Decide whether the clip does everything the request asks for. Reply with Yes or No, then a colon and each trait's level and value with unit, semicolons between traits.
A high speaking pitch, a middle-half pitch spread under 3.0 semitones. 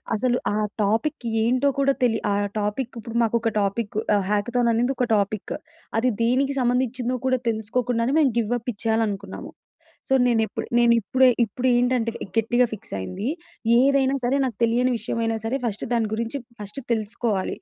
Yes: high, 235 Hz; narrow, 2.4 semitones